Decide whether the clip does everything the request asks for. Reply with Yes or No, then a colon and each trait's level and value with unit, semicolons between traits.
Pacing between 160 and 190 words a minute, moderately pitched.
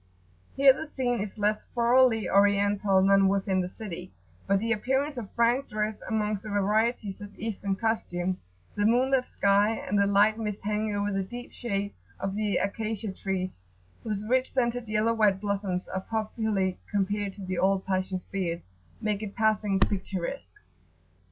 No: average, 165 wpm; high, 205 Hz